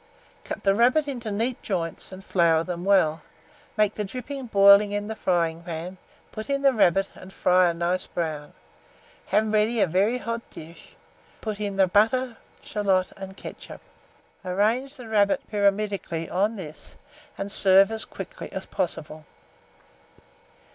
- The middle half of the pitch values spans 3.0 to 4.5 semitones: Yes, average, 3.5 semitones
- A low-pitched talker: No, high, 200 Hz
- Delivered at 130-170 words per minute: Yes, average, 150 wpm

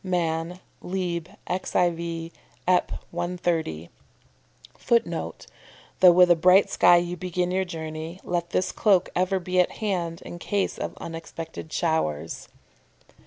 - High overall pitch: No, medium, 175 Hz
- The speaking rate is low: Yes, slow, 120 wpm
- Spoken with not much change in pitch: Yes, narrow, 1.7 semitones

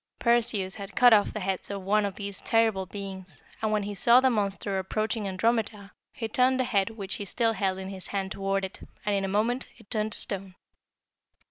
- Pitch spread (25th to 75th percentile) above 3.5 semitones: No, narrow, 2.5 semitones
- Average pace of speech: No, fast, 215 wpm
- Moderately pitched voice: No, high, 200 Hz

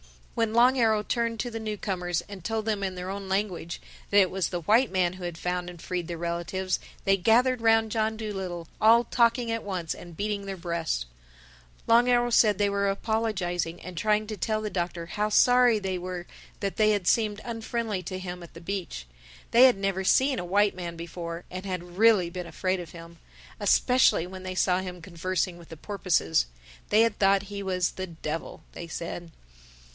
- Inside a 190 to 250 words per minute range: Yes, average, 195 wpm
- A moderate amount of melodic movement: Yes, average, 3.6 semitones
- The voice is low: No, high, 190 Hz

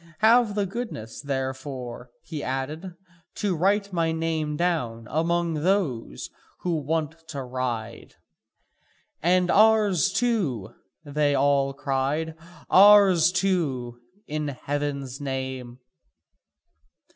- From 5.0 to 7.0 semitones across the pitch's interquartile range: Yes, average, 5.3 semitones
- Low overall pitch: No, medium, 155 Hz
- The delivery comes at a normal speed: No, slow, 100 wpm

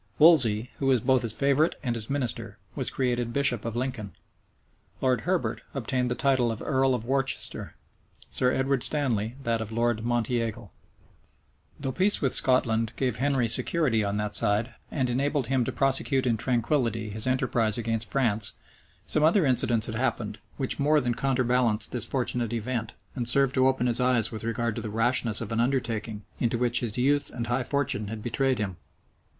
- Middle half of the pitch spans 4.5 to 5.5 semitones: No, average, 2.8 semitones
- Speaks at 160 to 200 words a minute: Yes, average, 180 wpm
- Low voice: Yes, low, 120 Hz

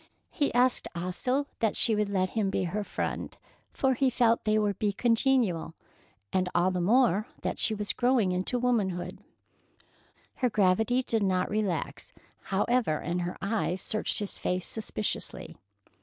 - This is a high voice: Yes, high, 210 Hz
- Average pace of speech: Yes, average, 155 wpm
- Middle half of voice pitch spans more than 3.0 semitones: Yes, average, 4.6 semitones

